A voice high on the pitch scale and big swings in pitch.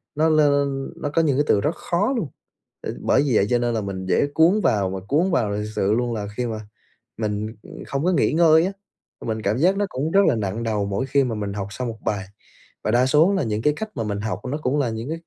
No: low, 125 Hz; wide, 6.3 semitones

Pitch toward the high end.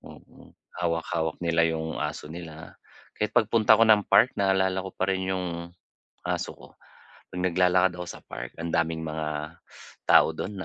No: very low, 85 Hz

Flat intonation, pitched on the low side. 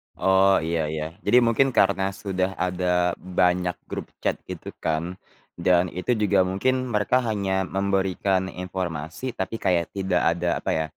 Yes: narrow, 1.8 semitones; very low, 95 Hz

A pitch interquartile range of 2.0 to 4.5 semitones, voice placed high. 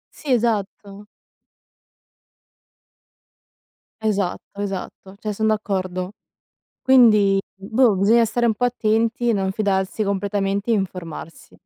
Yes: narrow, 2.4 semitones; high, 205 Hz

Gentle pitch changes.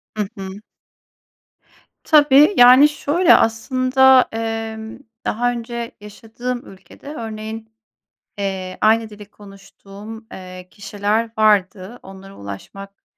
No: average, 3.6 semitones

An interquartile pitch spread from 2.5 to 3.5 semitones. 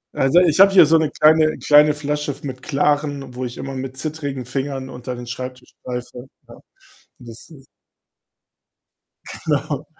Yes: average, 2.8 semitones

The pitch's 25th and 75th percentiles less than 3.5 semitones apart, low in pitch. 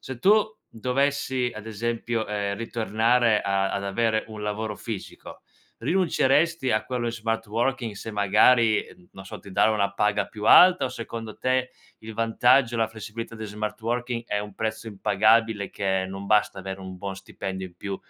Yes: average, 2.7 semitones; low, 110 Hz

